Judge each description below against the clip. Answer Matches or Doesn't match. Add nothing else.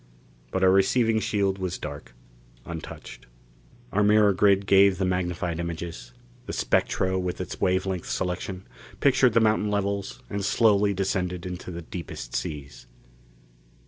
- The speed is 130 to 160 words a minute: Matches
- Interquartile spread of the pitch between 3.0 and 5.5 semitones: Doesn't match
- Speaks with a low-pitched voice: Matches